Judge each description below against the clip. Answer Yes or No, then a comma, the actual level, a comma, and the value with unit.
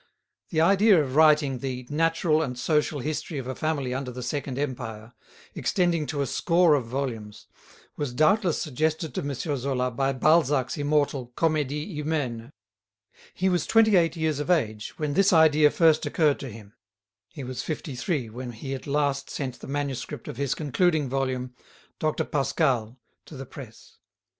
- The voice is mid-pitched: Yes, medium, 145 Hz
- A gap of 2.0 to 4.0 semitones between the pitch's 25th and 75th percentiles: Yes, average, 3.6 semitones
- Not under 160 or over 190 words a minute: Yes, average, 165 wpm